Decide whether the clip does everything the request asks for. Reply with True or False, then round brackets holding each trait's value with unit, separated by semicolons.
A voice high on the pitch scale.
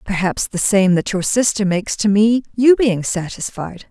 True (205 Hz)